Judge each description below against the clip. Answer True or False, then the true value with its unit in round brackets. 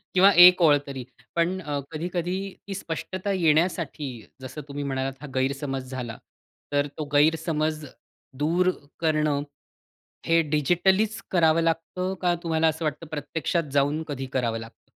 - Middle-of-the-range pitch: True (155 Hz)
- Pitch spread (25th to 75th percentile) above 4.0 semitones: False (3.4 semitones)